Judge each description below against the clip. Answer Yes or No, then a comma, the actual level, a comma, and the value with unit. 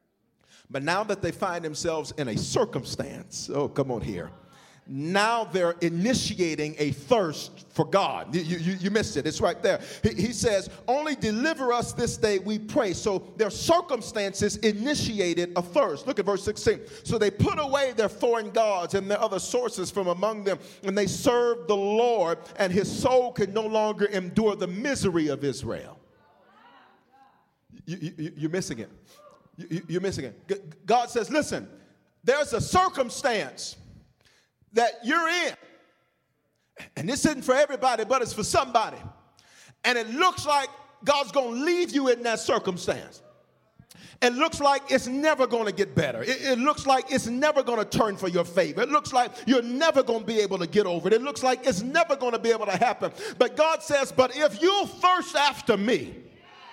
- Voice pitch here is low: No, high, 225 Hz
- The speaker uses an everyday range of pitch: No, wide, 5.7 semitones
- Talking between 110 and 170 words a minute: No, average, 180 wpm